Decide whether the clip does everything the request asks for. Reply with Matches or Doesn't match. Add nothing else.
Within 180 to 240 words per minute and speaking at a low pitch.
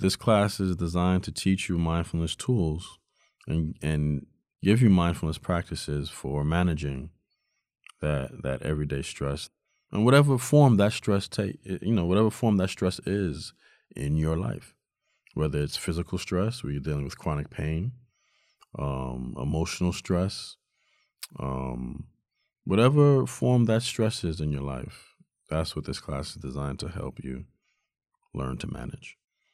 Doesn't match